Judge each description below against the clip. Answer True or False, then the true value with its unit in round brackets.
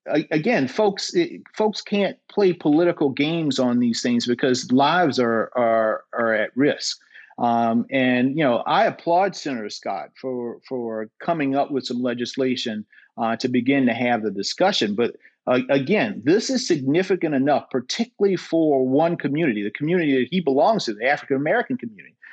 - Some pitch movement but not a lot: False (6.5 semitones)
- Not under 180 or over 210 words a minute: False (160 wpm)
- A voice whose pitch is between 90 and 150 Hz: True (135 Hz)